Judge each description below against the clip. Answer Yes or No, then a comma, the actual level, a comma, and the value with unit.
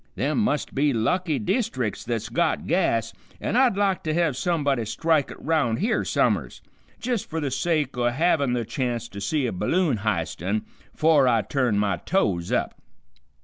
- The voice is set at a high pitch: No, medium, 140 Hz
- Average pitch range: No, wide, 6.5 semitones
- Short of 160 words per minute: No, average, 170 wpm